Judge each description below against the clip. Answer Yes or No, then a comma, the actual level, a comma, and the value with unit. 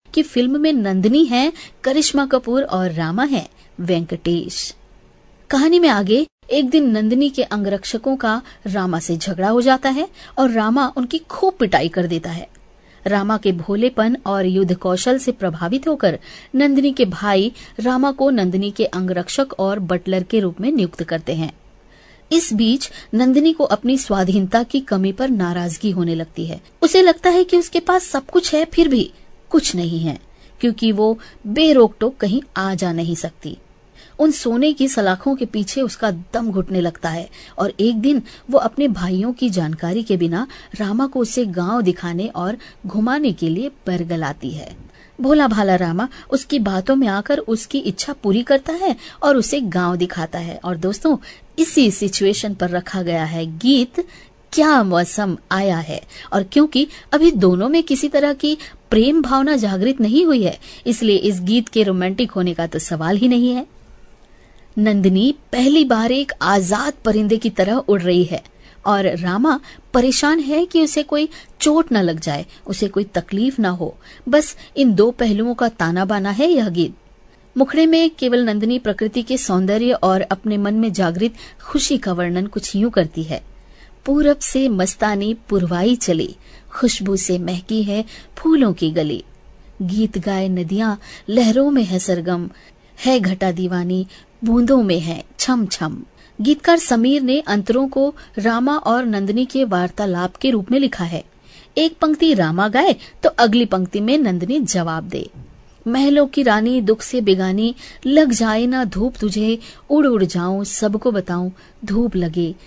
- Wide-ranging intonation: Yes, wide, 6.3 semitones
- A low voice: No, high, 220 Hz